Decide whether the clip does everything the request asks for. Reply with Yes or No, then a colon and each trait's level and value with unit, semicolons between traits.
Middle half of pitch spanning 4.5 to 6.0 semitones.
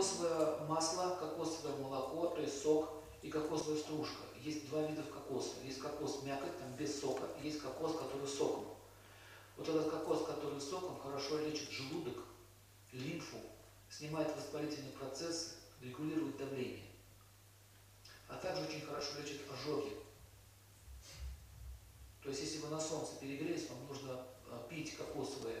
Yes: average, 5.2 semitones